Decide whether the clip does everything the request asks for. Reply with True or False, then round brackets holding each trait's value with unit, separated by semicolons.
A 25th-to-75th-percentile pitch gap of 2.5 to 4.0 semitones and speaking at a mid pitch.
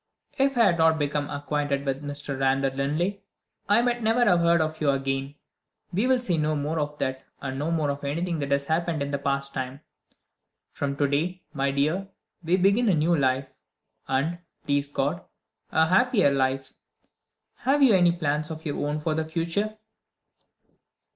True (3.7 semitones; 150 Hz)